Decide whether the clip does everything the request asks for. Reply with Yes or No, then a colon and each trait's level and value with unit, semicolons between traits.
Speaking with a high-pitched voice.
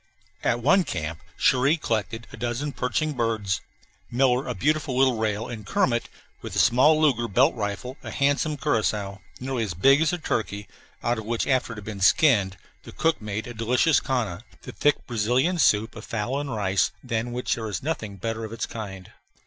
No: low, 120 Hz